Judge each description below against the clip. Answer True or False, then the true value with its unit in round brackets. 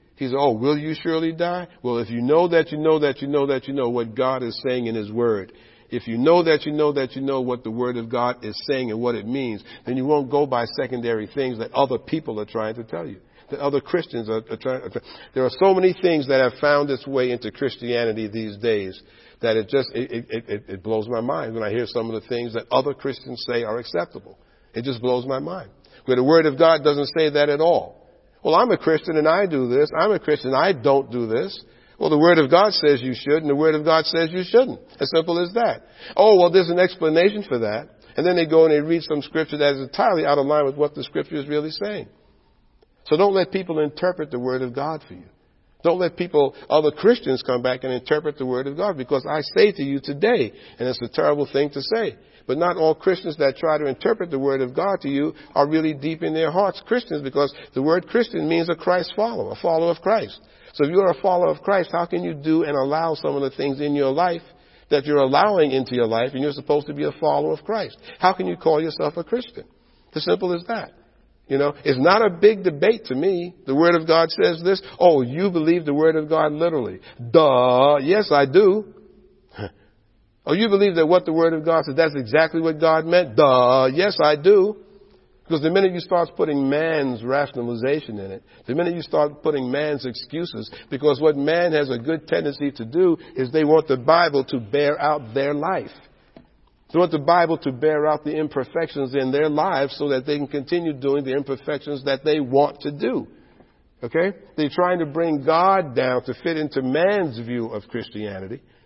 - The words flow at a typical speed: False (235 wpm)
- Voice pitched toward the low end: False (150 Hz)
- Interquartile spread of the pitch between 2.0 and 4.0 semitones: False (4.4 semitones)